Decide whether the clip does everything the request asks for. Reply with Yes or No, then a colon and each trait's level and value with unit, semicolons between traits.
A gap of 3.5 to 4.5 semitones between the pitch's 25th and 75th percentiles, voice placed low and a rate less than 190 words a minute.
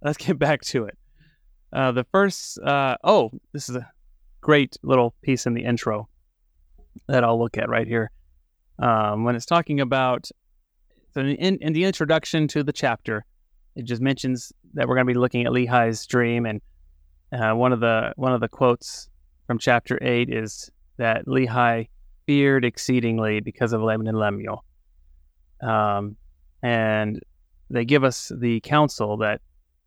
Yes: average, 4.1 semitones; low, 120 Hz; average, 165 wpm